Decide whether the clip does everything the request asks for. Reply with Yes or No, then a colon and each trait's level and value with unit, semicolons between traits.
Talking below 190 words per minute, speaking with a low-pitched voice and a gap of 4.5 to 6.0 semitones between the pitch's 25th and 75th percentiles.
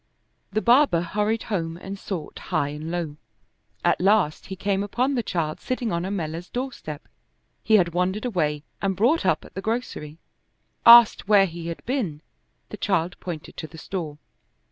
No: average, 165 wpm; medium, 185 Hz; average, 4.8 semitones